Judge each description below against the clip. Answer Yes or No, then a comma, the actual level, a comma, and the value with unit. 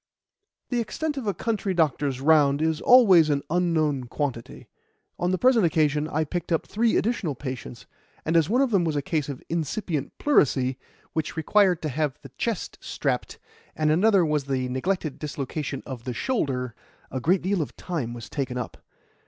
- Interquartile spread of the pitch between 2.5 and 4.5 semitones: No, average, 5.2 semitones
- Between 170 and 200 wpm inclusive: Yes, average, 175 wpm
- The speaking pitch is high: No, medium, 155 Hz